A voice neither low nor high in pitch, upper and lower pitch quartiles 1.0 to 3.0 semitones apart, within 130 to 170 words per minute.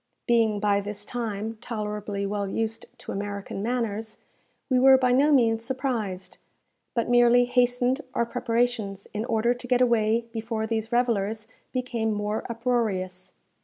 No: high, 225 Hz; average, 2.7 semitones; average, 140 wpm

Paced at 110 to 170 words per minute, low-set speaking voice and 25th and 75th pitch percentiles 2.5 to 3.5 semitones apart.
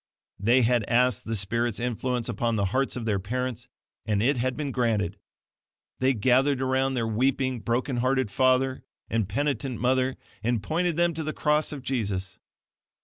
Yes: average, 165 wpm; low, 125 Hz; average, 2.8 semitones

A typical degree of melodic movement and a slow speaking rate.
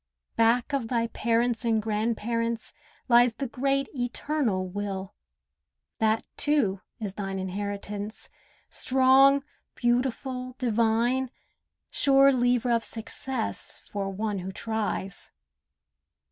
Yes: average, 3.4 semitones; slow, 100 wpm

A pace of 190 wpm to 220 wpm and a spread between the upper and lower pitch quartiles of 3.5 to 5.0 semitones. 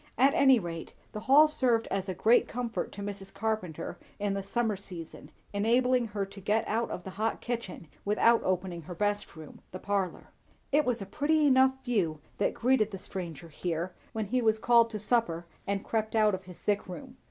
Yes: average, 200 wpm; average, 4.1 semitones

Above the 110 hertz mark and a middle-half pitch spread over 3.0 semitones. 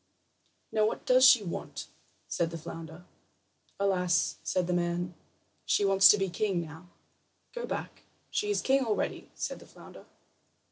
Yes: medium, 185 Hz; average, 3.8 semitones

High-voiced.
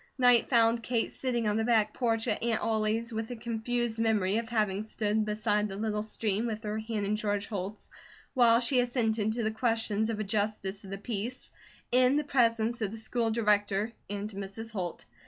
Yes: high, 220 Hz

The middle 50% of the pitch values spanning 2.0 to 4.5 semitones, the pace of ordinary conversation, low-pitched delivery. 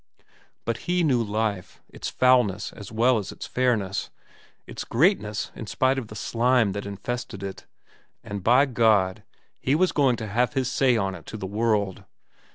Yes: average, 3.9 semitones; average, 170 wpm; low, 115 Hz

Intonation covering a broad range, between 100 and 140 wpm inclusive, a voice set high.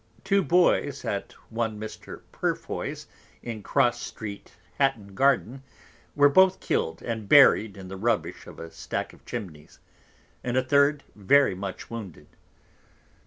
No: wide, 5.7 semitones; slow, 135 wpm; low, 115 Hz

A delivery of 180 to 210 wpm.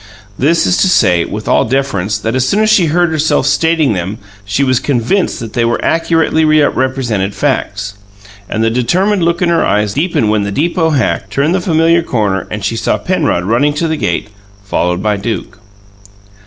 Yes: average, 185 wpm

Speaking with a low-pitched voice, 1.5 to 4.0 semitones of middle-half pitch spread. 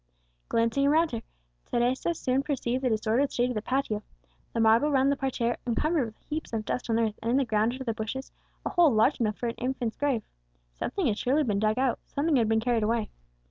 No: high, 245 Hz; average, 3.5 semitones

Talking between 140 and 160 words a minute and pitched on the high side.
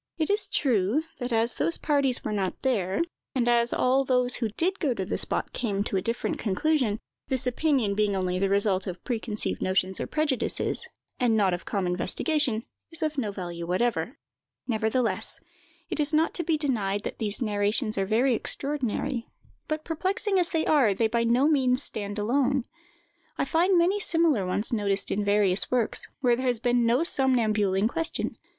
No: average, 185 wpm; high, 235 Hz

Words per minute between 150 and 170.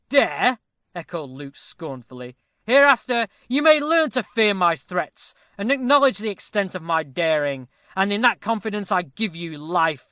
Yes: average, 160 wpm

